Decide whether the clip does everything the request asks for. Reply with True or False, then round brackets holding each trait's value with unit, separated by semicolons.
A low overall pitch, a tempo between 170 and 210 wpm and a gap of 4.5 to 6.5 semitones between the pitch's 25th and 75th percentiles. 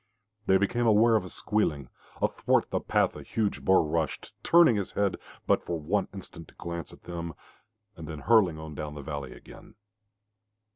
True (85 Hz; 180 wpm; 5.0 semitones)